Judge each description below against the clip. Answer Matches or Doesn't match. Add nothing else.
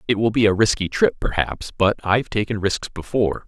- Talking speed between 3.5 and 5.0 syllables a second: Doesn't match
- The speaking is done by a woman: Doesn't match